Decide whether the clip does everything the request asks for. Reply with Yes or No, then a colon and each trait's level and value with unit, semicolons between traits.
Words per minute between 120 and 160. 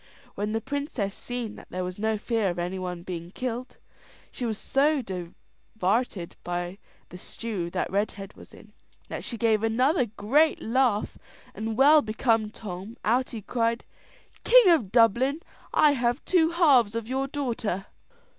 Yes: average, 155 wpm